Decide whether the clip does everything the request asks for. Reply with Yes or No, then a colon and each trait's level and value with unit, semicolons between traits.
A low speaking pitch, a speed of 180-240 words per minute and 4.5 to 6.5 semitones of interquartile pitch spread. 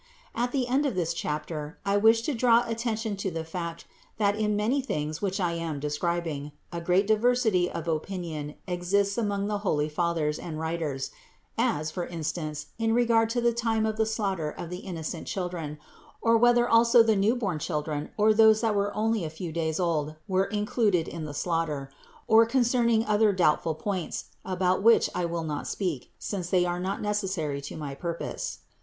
No: medium, 185 Hz; average, 190 wpm; wide, 5.4 semitones